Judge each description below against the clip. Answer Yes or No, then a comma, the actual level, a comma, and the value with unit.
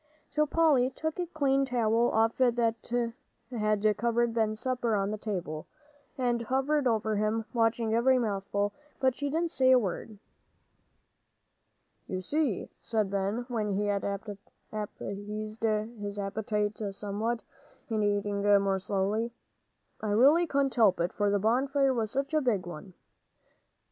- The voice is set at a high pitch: Yes, high, 220 Hz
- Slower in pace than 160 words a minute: Yes, average, 140 wpm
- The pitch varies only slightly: No, average, 3.5 semitones